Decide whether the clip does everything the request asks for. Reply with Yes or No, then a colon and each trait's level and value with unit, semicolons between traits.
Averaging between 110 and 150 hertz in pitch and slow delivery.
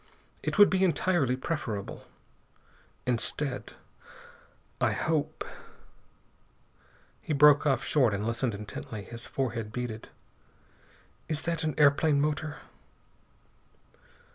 Yes: medium, 140 Hz; slow, 100 wpm